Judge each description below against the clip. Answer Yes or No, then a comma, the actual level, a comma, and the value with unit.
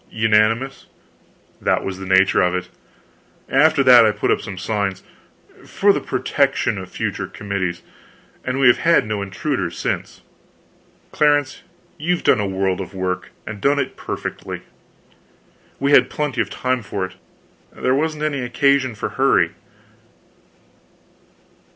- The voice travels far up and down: Yes, wide, 6.2 semitones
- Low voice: Yes, low, 115 Hz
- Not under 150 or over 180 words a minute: No, average, 140 wpm